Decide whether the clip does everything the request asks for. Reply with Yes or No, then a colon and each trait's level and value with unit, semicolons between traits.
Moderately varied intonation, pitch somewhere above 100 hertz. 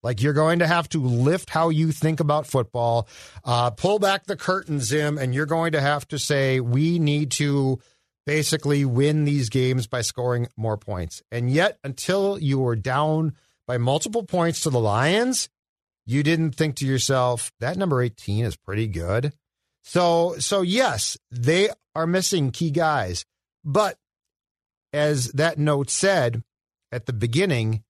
Yes: average, 4.9 semitones; medium, 140 Hz